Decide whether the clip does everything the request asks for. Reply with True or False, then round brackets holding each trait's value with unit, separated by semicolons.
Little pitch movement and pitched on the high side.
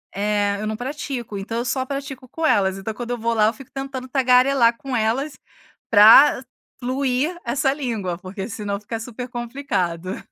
False (4.2 semitones; 240 Hz)